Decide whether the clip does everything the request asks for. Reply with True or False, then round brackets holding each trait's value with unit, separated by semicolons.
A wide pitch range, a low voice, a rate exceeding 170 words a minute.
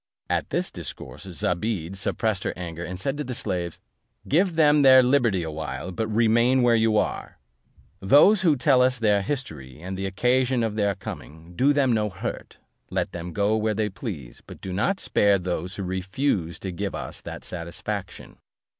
True (5.8 semitones; 105 Hz; 180 wpm)